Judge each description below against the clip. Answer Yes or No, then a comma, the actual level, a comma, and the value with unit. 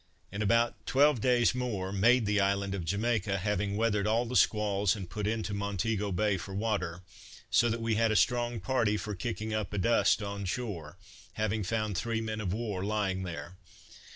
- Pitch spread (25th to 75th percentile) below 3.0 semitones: Yes, narrow, 2.5 semitones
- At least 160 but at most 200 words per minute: Yes, average, 185 wpm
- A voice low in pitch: Yes, low, 105 Hz